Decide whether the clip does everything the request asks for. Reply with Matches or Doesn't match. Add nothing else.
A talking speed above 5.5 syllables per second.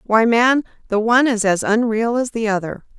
Doesn't match